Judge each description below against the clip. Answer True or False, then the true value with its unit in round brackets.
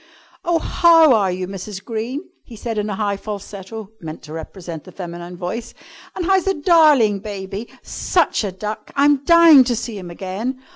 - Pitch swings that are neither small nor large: False (6.6 semitones)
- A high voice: True (215 Hz)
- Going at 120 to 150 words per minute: False (180 wpm)